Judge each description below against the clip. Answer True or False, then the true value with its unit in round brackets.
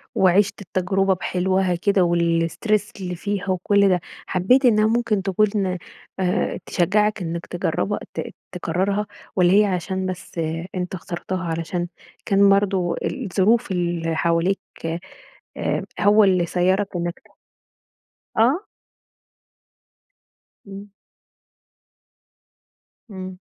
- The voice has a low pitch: False (185 Hz)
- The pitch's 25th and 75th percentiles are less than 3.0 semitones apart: True (2.4 semitones)